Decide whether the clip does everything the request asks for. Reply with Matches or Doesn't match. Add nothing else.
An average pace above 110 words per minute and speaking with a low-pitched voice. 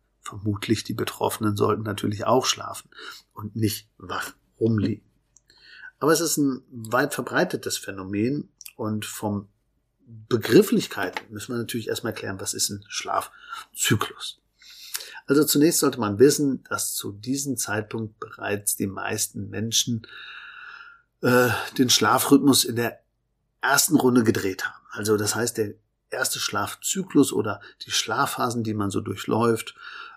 Matches